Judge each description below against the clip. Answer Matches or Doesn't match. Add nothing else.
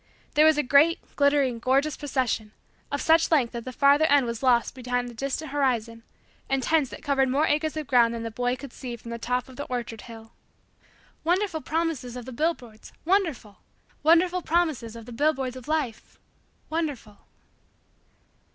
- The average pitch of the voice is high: Matches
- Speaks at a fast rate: Doesn't match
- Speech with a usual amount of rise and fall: Matches